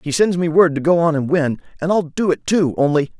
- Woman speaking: No, male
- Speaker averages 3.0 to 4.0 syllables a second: No, 5.6 syllables/s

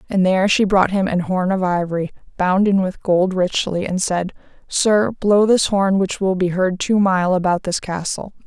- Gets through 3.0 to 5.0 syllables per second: Yes, 4.6 syllables/s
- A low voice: No, high, 190 Hz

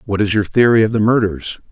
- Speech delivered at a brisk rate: Yes, fast, 245 wpm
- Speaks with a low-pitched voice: Yes, low, 105 Hz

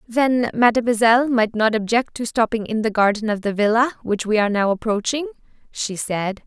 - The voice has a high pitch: Yes, high, 225 Hz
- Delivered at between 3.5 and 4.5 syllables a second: No, 5.4 syllables/s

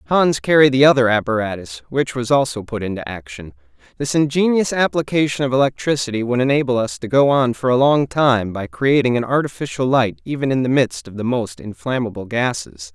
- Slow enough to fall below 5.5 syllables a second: No, 5.6 syllables/s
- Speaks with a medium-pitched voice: No, low, 125 Hz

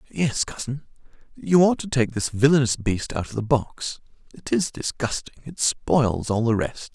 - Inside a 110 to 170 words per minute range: Yes, average, 165 wpm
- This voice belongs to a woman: No, male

